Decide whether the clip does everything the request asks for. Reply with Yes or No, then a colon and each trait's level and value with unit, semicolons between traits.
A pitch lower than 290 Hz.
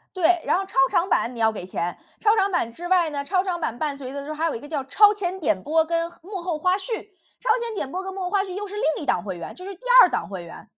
No: very high, 340 Hz